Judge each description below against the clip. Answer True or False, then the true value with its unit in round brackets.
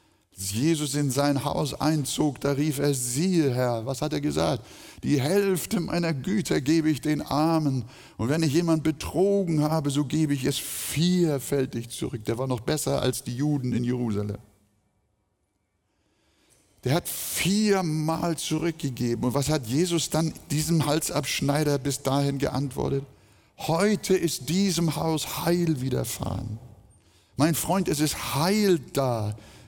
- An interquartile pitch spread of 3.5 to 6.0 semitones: True (4.7 semitones)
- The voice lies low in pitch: False (145 Hz)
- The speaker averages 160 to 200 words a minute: False (140 wpm)